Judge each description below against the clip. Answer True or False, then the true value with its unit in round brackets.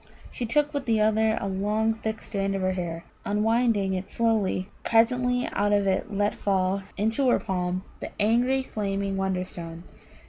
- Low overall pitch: False (205 Hz)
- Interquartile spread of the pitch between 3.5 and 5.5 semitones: False (2.9 semitones)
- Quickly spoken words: False (170 wpm)